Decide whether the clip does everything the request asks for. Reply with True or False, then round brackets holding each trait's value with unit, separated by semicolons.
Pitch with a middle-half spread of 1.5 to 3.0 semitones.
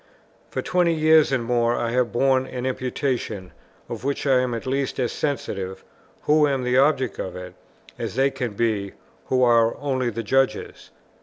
True (2.7 semitones)